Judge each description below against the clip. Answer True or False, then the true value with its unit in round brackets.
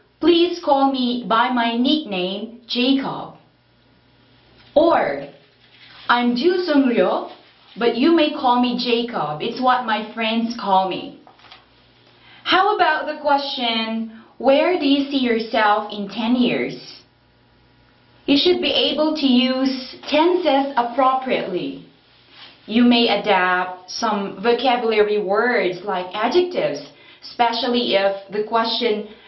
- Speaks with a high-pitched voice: True (240 Hz)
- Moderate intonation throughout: True (4.2 semitones)